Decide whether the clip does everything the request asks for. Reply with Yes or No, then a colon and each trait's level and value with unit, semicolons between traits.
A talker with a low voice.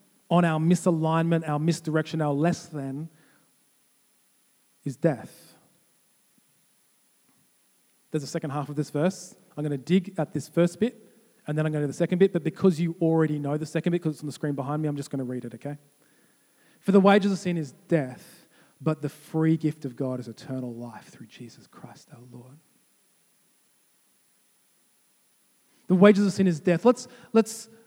No: medium, 160 Hz